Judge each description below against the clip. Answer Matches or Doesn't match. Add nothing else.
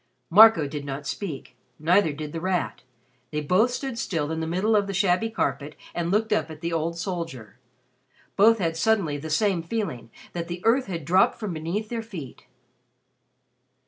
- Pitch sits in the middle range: Matches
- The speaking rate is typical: Matches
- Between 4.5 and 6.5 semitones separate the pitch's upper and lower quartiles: Matches